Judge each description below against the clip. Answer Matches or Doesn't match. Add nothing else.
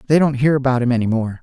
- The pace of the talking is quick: Matches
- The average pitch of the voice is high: Doesn't match